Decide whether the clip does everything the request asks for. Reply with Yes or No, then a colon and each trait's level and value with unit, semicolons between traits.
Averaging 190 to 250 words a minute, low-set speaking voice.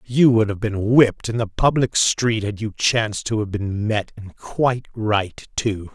Yes: average, 200 wpm; low, 110 Hz